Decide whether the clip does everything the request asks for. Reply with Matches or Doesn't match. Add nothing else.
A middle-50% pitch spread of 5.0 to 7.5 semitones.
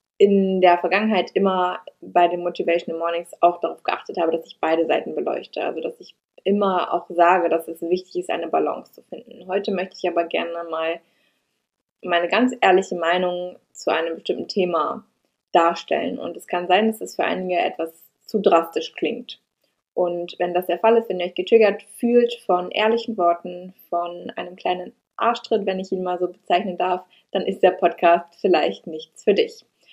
Doesn't match